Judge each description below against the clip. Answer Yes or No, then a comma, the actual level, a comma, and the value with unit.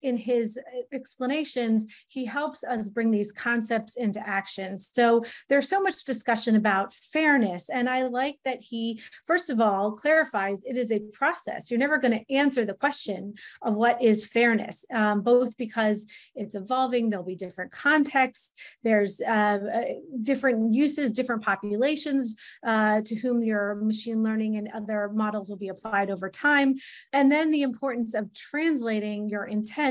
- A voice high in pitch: Yes, high, 230 Hz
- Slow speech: No, average, 160 wpm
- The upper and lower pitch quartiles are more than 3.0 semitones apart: Yes, average, 3.8 semitones